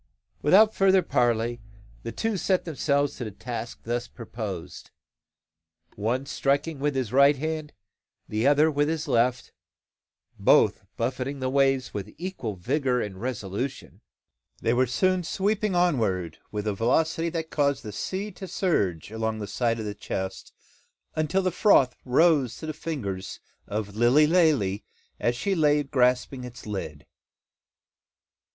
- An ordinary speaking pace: Yes, average, 145 wpm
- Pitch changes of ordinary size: No, wide, 6.0 semitones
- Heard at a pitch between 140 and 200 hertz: No, low, 130 Hz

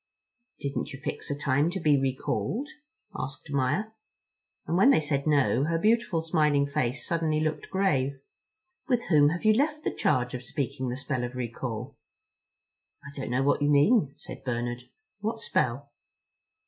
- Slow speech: No, average, 160 wpm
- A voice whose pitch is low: No, medium, 145 Hz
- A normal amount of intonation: Yes, average, 4.3 semitones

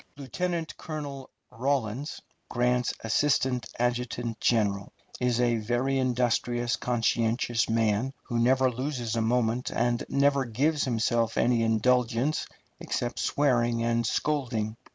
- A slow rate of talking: Yes, slow, 110 wpm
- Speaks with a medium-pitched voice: No, low, 120 Hz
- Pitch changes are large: No, narrow, 2.4 semitones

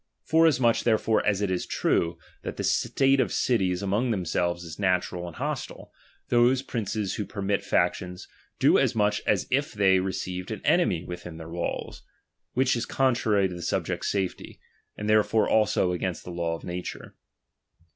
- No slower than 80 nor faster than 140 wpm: No, average, 165 wpm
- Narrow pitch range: No, average, 4.2 semitones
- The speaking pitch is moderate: No, low, 100 Hz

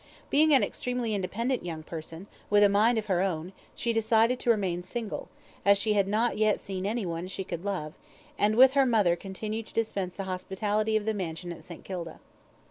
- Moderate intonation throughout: Yes, average, 3.4 semitones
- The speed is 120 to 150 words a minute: No, average, 200 wpm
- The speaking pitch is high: Yes, high, 205 Hz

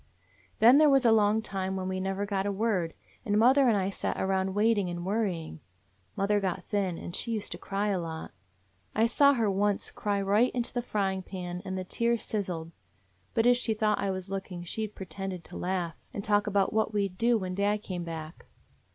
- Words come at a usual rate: No, fast, 220 wpm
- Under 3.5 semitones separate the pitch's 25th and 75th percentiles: Yes, narrow, 2.6 semitones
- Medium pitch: No, high, 200 Hz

